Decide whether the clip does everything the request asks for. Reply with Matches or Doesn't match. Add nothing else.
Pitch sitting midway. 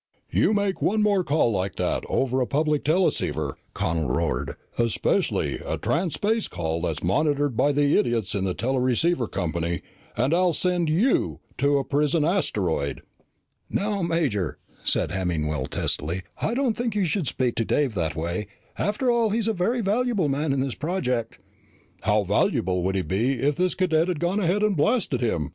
Matches